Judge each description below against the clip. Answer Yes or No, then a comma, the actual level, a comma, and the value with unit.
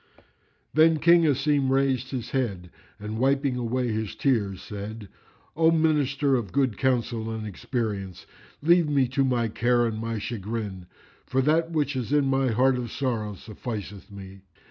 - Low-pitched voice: Yes, low, 125 Hz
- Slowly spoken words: No, average, 155 wpm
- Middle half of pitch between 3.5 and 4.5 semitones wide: Yes, average, 4.2 semitones